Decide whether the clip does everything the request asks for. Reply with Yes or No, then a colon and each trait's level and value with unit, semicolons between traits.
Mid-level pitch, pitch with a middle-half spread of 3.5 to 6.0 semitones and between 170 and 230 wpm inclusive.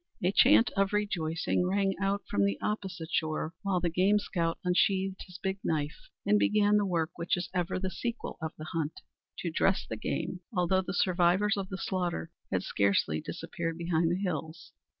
No: medium, 180 Hz; average, 3.1 semitones; average, 185 wpm